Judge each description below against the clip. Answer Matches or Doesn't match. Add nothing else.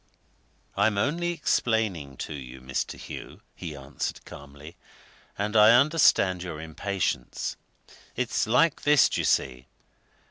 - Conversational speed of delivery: Doesn't match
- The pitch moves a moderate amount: Doesn't match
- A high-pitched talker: Doesn't match